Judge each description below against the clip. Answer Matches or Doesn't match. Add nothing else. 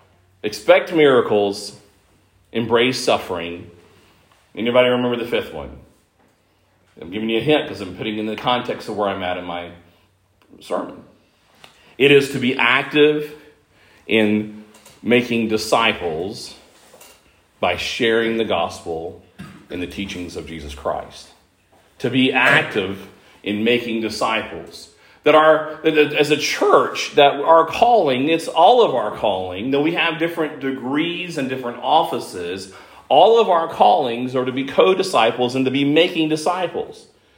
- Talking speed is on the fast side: Doesn't match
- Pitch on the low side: Matches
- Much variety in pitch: Matches